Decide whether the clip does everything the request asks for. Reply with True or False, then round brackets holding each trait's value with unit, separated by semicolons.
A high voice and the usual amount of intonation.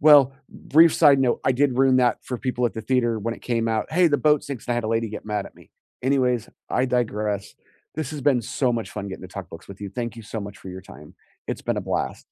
False (120 Hz; 3.9 semitones)